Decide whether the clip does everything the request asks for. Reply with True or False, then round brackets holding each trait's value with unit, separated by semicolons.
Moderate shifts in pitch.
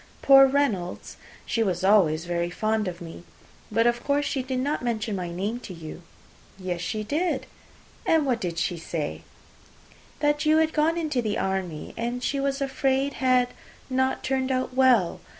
False (6.8 semitones)